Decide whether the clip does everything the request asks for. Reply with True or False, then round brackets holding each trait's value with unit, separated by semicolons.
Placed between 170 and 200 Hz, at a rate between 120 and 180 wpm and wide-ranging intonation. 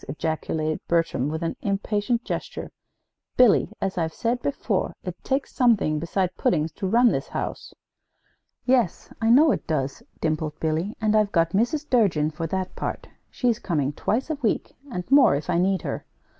True (190 Hz; 170 wpm; 6.7 semitones)